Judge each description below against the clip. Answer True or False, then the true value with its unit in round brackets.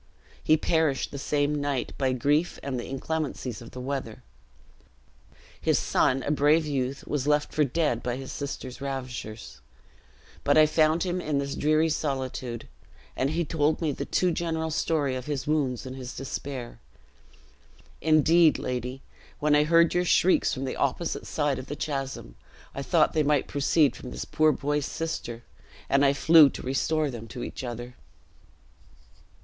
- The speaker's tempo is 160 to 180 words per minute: True (165 wpm)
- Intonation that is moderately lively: True (3.1 semitones)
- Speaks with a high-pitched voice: False (140 Hz)